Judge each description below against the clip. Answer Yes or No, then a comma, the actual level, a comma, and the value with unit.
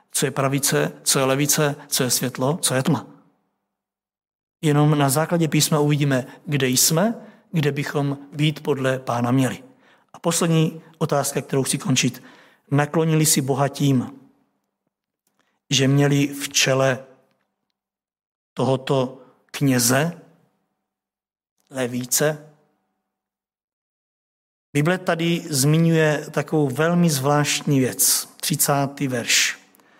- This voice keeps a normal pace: No, slow, 100 wpm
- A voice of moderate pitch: Yes, medium, 145 Hz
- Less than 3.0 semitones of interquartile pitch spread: Yes, narrow, 2.6 semitones